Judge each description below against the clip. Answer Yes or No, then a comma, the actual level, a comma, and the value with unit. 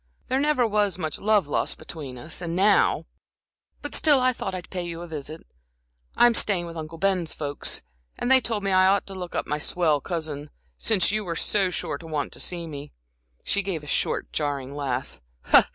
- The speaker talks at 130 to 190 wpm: No, average, 200 wpm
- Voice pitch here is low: No, medium, 175 Hz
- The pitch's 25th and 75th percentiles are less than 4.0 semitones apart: No, average, 4.6 semitones